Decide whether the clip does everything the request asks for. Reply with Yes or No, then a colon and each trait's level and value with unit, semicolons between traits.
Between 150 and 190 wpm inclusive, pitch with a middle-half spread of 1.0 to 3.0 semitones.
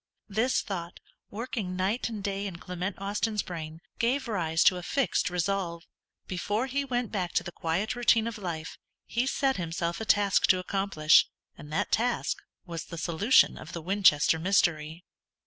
No: average, 165 wpm; average, 4.6 semitones